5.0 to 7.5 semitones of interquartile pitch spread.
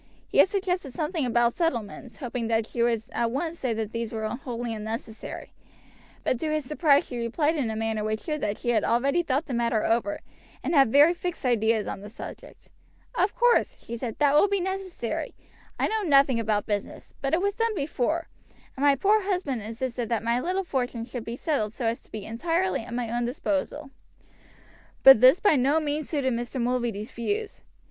Yes: average, 5.3 semitones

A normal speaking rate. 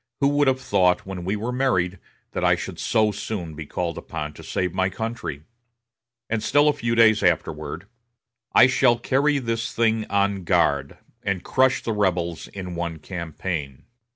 Yes: average, 170 wpm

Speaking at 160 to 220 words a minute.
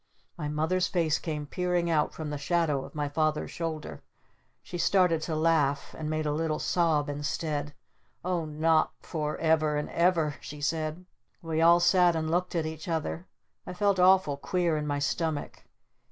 Yes: average, 170 wpm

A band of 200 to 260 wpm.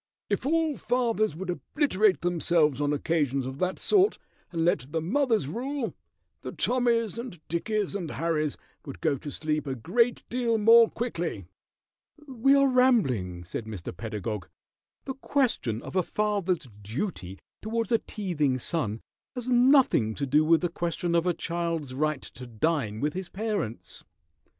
No: average, 155 wpm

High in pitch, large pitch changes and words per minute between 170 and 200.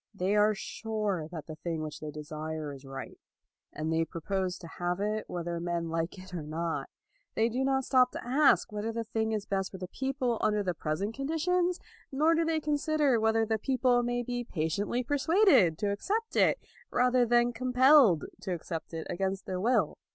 Yes: high, 210 Hz; wide, 6.7 semitones; average, 190 wpm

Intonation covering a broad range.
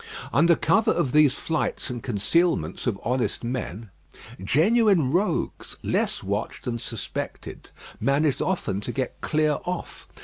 Yes: wide, 5.7 semitones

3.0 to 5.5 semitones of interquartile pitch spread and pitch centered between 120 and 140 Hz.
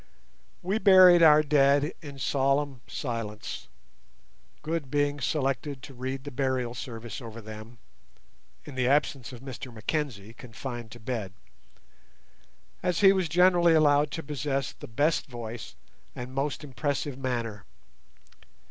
Yes: average, 3.7 semitones; low, 135 Hz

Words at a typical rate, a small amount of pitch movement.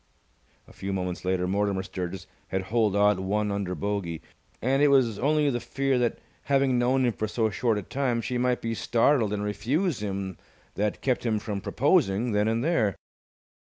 No: average, 185 wpm; average, 4.1 semitones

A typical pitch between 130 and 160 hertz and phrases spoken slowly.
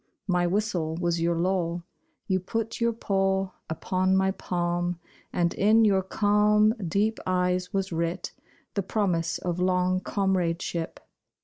No: medium, 185 Hz; slow, 130 wpm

